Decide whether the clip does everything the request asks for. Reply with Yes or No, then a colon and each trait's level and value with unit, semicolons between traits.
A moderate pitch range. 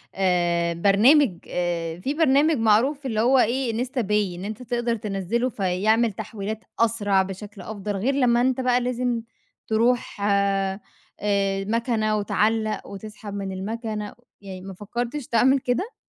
Yes: average, 3.7 semitones